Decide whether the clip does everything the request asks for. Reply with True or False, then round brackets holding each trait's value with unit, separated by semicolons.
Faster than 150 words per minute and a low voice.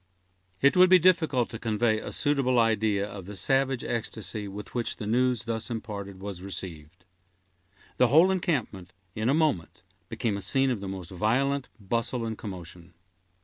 True (165 wpm; 110 Hz)